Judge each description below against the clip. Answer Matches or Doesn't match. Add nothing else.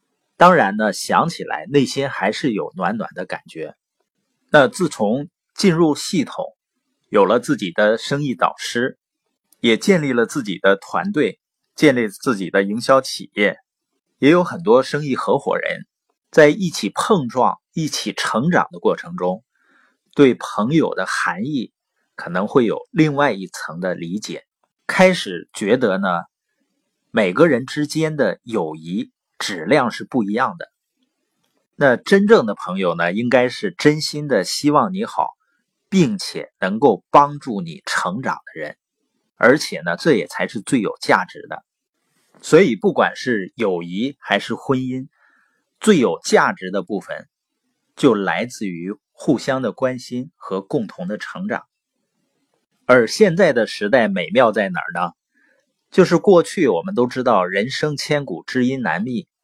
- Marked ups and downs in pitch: Matches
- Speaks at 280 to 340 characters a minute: Doesn't match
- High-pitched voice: Doesn't match